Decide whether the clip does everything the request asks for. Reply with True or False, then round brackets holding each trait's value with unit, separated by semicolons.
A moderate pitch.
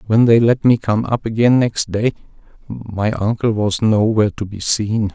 False (110 Hz)